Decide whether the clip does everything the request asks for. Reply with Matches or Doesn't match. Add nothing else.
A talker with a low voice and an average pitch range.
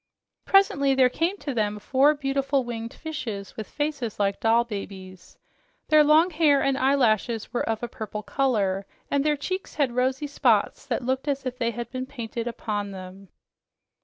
Doesn't match